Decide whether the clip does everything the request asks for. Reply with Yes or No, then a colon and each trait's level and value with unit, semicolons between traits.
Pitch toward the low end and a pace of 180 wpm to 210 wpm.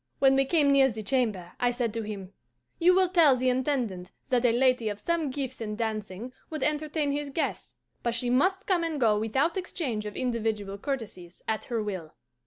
No: very high, 250 Hz; average, 195 wpm